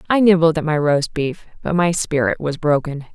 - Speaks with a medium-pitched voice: Yes, medium, 160 Hz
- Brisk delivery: Yes, fast, 210 wpm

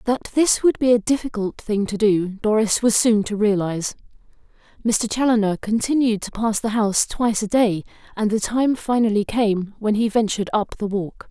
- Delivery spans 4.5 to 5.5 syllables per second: Yes, 5.1 syllables/s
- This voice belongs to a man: No, female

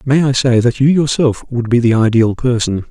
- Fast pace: Yes, fast, 225 wpm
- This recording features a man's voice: Yes, male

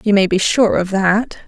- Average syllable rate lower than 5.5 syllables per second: Yes, 4.6 syllables/s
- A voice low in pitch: No, high, 200 Hz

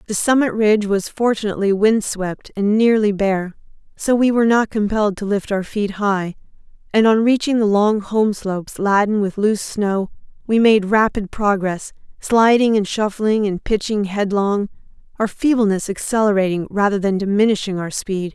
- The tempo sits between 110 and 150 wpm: No, average, 160 wpm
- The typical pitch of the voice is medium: No, high, 205 Hz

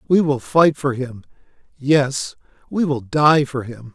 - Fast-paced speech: No, average, 165 wpm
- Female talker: No, male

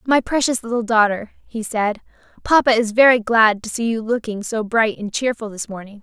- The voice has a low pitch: No, high, 225 Hz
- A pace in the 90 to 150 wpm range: No, average, 200 wpm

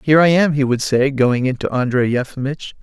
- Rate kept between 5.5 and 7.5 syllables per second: Yes, 5.6 syllables/s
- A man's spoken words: Yes, male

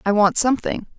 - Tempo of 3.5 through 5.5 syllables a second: No, 6.3 syllables/s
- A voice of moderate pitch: No, high, 215 Hz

